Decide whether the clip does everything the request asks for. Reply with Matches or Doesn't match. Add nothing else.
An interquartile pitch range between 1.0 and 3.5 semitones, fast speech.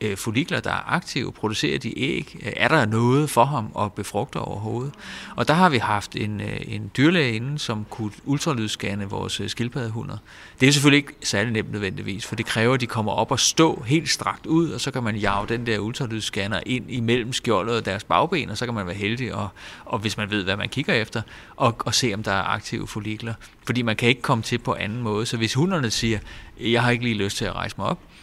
Matches